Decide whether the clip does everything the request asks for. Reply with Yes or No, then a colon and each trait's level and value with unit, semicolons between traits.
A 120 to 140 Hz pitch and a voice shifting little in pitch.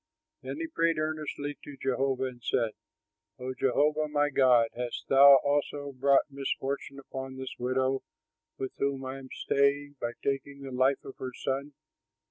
Yes: low, 135 Hz; narrow, 1.5 semitones